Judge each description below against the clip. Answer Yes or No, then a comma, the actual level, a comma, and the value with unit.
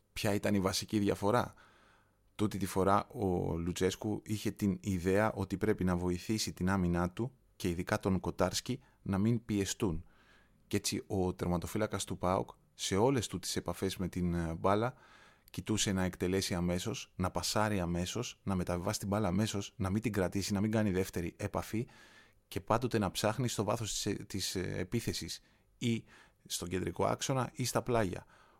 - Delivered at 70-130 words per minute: No, average, 160 wpm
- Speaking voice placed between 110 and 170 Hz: No, low, 100 Hz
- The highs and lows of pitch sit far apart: No, average, 2.9 semitones